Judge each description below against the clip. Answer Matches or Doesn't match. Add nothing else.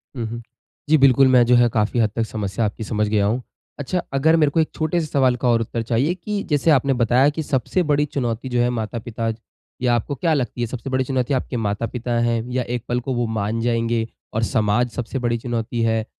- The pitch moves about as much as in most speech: Matches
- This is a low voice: Matches